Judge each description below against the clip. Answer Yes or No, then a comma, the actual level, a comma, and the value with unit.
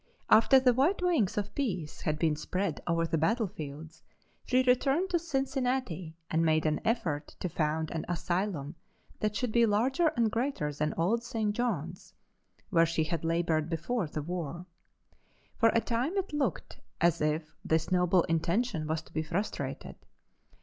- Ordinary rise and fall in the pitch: No, wide, 7.0 semitones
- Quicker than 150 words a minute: Yes, average, 160 wpm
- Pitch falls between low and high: Yes, medium, 180 Hz